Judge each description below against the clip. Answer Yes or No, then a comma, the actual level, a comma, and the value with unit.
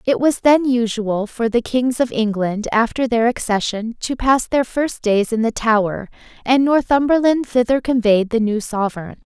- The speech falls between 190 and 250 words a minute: No, average, 175 wpm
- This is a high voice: Yes, high, 235 Hz